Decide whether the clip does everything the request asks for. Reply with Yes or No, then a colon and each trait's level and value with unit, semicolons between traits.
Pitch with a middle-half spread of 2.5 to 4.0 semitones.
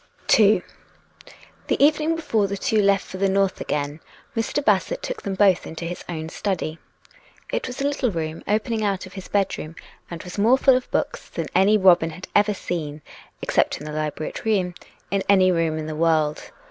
No: average, 4.7 semitones